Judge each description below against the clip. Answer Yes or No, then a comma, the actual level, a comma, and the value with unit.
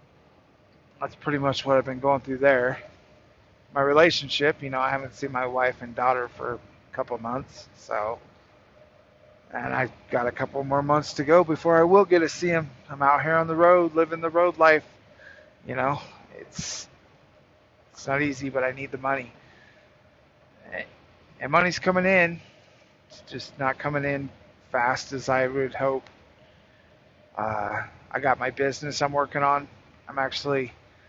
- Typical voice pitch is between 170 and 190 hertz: No, low, 135 Hz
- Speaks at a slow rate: No, average, 165 wpm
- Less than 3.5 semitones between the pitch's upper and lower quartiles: Yes, average, 3.1 semitones